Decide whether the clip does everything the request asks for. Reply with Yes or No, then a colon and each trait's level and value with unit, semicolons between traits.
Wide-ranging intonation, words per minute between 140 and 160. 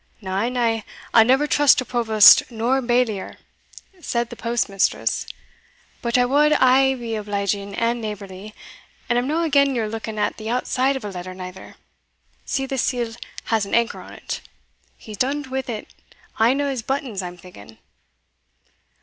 No: average, 3.9 semitones; average, 155 wpm